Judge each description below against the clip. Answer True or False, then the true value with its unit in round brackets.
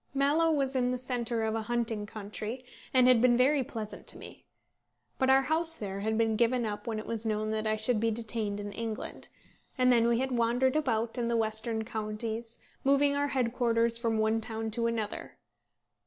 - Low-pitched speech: False (230 Hz)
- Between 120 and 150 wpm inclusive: False (200 wpm)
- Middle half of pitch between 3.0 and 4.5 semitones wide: False (2.5 semitones)